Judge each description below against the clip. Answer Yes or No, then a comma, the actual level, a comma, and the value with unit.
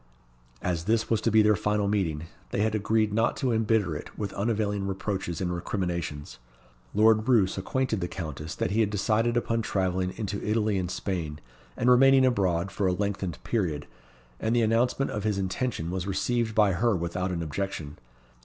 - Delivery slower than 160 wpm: No, average, 180 wpm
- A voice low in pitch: Yes, low, 100 Hz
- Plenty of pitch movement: No, average, 3.5 semitones